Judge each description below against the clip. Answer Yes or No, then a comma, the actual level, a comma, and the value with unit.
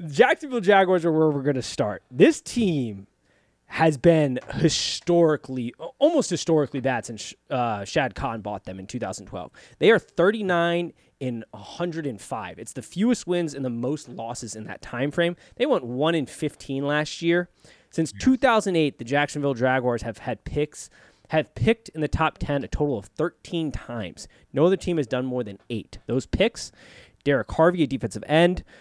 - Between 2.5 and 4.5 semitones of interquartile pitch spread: No, average, 5.3 semitones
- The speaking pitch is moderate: Yes, medium, 150 Hz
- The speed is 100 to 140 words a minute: No, average, 175 wpm